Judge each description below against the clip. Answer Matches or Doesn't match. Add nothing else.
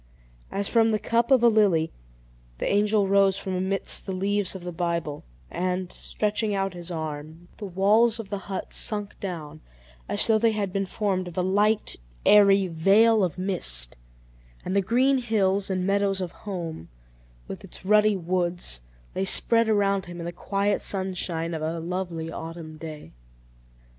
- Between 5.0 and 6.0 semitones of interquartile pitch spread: Doesn't match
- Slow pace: Doesn't match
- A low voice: Doesn't match